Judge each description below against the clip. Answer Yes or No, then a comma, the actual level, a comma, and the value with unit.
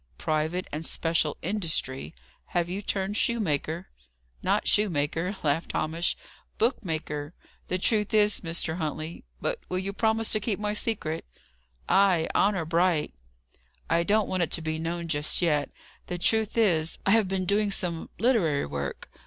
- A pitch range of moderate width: Yes, average, 4.5 semitones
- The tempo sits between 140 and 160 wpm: Yes, average, 155 wpm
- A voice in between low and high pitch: Yes, medium, 175 Hz